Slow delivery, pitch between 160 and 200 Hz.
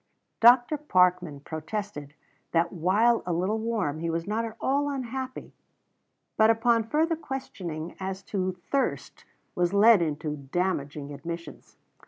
Yes: slow, 130 wpm; high, 190 Hz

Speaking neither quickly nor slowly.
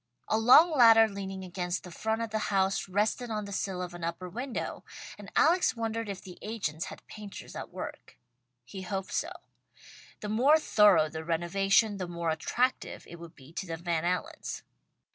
Yes: average, 180 wpm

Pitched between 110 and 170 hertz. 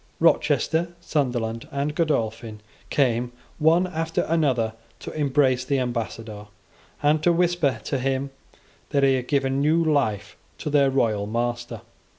Yes: low, 135 Hz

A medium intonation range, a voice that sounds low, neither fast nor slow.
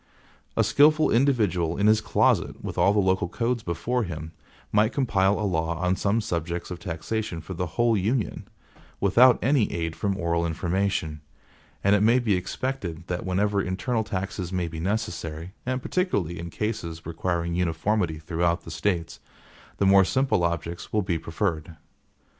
Yes: average, 4.2 semitones; very low, 95 Hz; average, 160 wpm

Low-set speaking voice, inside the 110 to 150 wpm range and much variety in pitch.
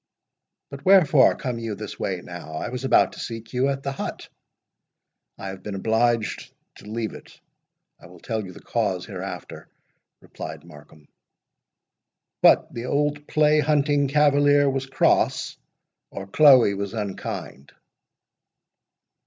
Yes: low, 120 Hz; slow, 135 wpm; wide, 6.1 semitones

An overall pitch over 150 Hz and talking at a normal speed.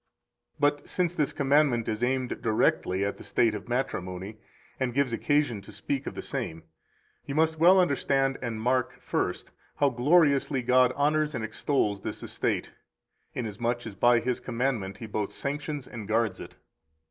No: low, 125 Hz; average, 165 wpm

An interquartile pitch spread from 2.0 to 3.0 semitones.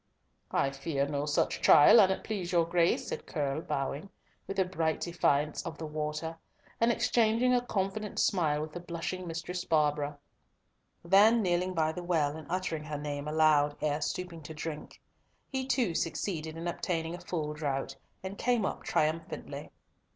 No: average, 3.4 semitones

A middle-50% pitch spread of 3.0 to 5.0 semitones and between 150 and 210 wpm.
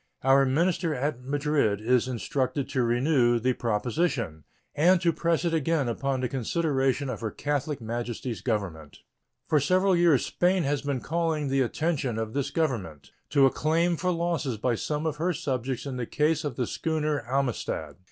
Yes: average, 4.6 semitones; average, 170 wpm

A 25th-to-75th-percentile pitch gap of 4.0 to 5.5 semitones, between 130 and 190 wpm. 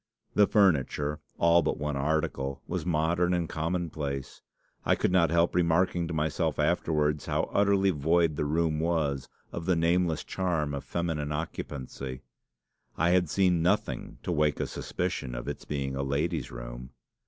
No: average, 3.1 semitones; average, 155 wpm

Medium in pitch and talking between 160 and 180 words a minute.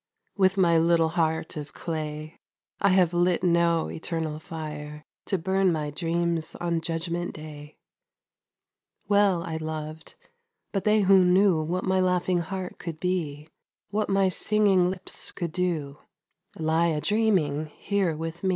No: medium, 170 Hz; average, 140 wpm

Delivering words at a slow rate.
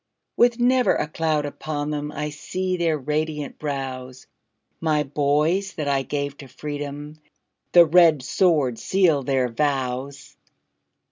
Yes: slow, 130 wpm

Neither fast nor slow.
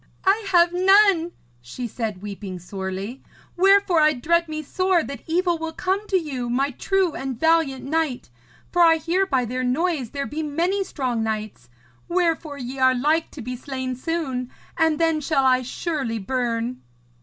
Yes: average, 165 wpm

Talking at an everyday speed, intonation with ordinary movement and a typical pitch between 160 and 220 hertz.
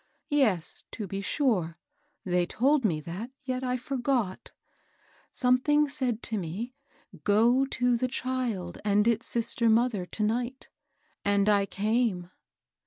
No: average, 150 wpm; average, 4.3 semitones; high, 230 Hz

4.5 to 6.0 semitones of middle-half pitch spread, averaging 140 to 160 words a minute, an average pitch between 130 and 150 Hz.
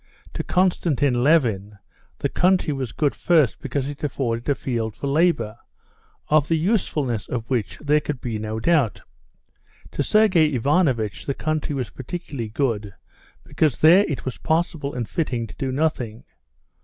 Yes: average, 5.1 semitones; average, 155 wpm; medium, 140 Hz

